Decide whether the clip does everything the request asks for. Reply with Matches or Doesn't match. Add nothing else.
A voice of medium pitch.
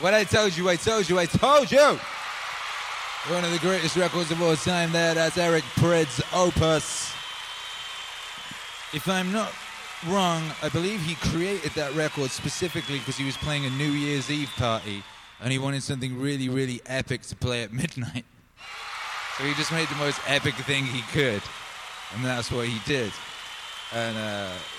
Matches